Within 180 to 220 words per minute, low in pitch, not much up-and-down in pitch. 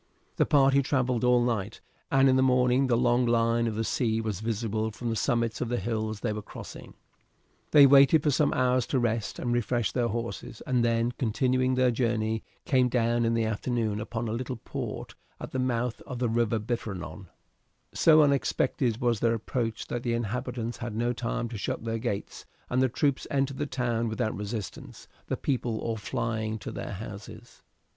Yes: average, 190 wpm; low, 120 Hz; narrow, 2.2 semitones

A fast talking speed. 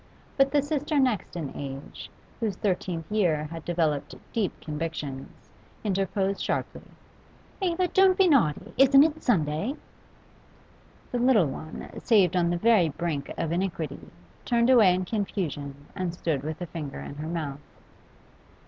No: average, 140 wpm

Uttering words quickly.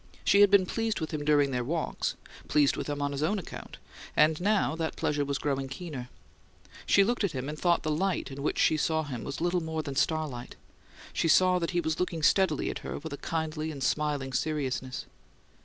Yes: fast, 215 wpm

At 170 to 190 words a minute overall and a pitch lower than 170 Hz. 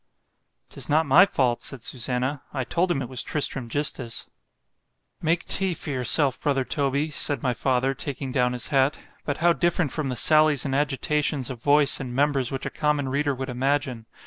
Yes: average, 175 wpm; medium, 140 Hz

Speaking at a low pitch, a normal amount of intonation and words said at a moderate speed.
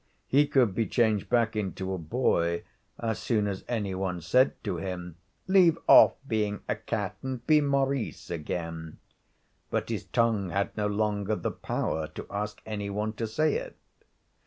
Yes: low, 105 Hz; average, 4.0 semitones; average, 165 wpm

